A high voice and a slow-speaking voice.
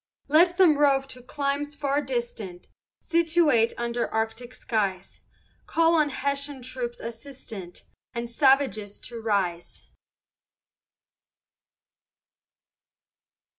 Yes: very high, 255 Hz; slow, 95 wpm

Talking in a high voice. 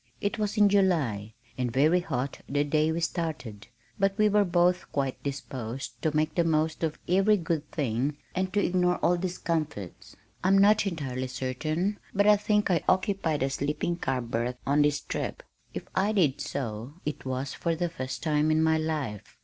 No: medium, 155 Hz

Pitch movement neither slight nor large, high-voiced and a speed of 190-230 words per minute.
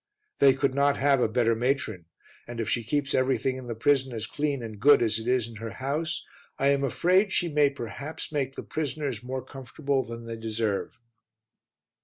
No: average, 3.5 semitones; low, 130 Hz; average, 195 wpm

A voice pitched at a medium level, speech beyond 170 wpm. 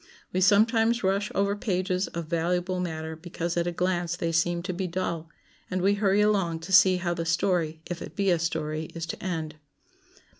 Yes: medium, 175 Hz; average, 195 wpm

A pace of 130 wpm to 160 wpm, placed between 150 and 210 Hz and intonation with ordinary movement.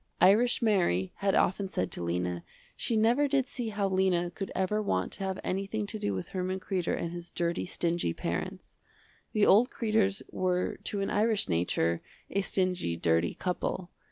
No: average, 175 wpm; high, 190 Hz; average, 3.7 semitones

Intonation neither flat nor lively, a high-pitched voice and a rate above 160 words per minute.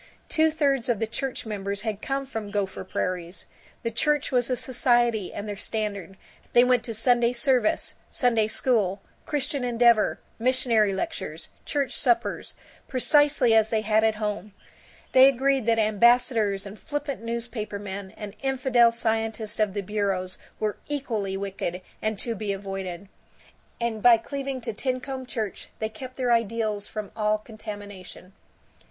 No: average, 3.4 semitones; high, 225 Hz; average, 145 wpm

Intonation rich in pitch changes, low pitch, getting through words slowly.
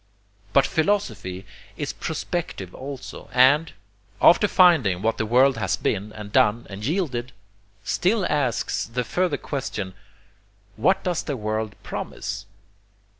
Yes: wide, 6.9 semitones; low, 125 Hz; slow, 125 wpm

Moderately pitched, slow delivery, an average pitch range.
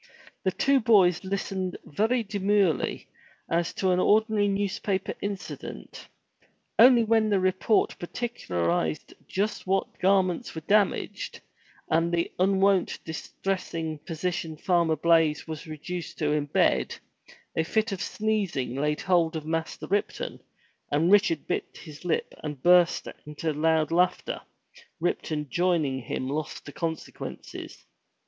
Yes: medium, 175 Hz; slow, 125 wpm; average, 4.0 semitones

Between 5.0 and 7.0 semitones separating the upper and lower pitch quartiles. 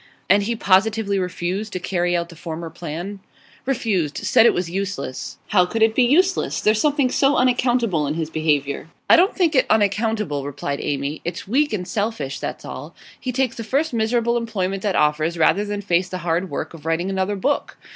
Yes: wide, 5.4 semitones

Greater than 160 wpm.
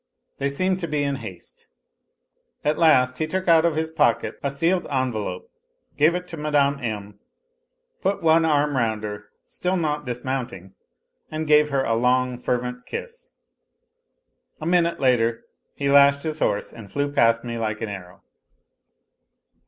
No: average, 155 wpm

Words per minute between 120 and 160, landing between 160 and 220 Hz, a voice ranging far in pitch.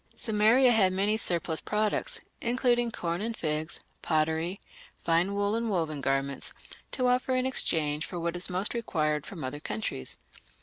Yes: average, 155 wpm; medium, 185 Hz; wide, 6.0 semitones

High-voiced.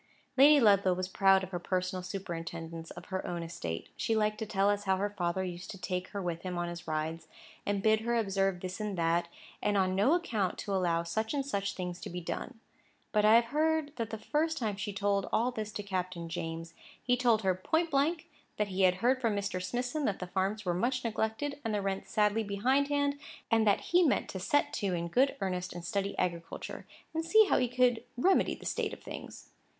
Yes: high, 200 Hz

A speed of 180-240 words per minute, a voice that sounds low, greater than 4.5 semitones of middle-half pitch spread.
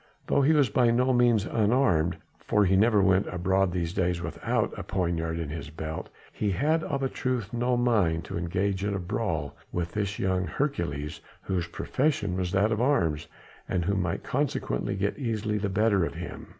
Yes: average, 190 wpm; very low, 95 Hz; average, 5.2 semitones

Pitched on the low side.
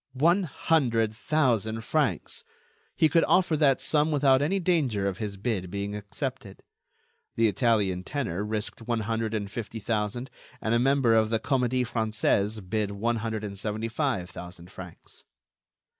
Yes: low, 115 Hz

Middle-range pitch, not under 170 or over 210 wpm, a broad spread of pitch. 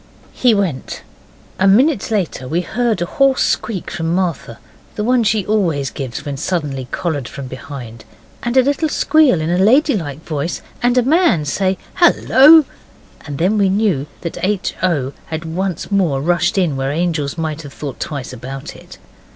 Yes: medium, 175 Hz; average, 175 wpm; wide, 7.0 semitones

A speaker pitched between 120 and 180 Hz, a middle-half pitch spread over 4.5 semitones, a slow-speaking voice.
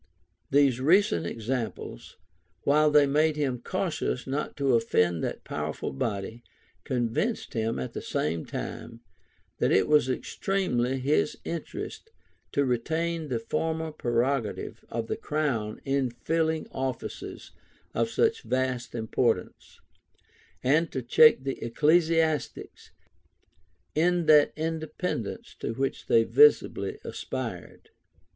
Yes: low, 135 Hz; average, 5.2 semitones; slow, 115 wpm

